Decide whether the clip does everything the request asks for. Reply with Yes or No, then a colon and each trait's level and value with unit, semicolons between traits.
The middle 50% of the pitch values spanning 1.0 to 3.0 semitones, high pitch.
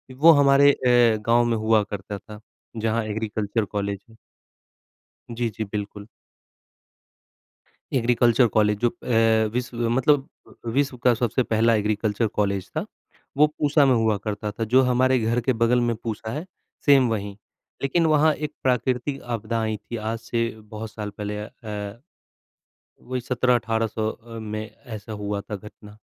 No: average, 2.7 semitones; low, 115 Hz